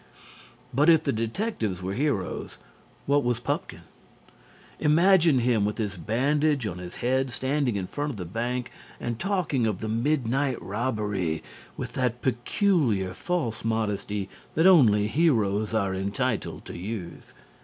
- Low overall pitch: Yes, low, 120 Hz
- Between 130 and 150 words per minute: Yes, average, 140 wpm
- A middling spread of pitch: No, wide, 5.7 semitones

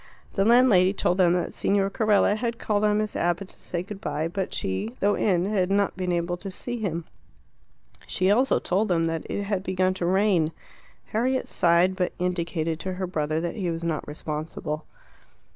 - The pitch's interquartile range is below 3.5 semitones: Yes, average, 3.1 semitones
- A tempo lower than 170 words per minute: No, average, 190 wpm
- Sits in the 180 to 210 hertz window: Yes, medium, 185 Hz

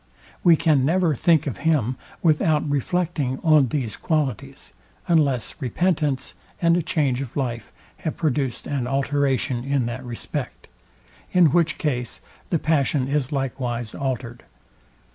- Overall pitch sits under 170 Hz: Yes, medium, 140 Hz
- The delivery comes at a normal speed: No, slow, 130 wpm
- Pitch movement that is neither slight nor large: Yes, average, 3.6 semitones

